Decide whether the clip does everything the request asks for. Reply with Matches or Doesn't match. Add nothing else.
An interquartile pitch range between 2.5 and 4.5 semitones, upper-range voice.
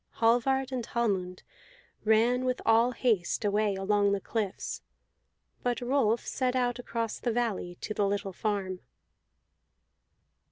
Matches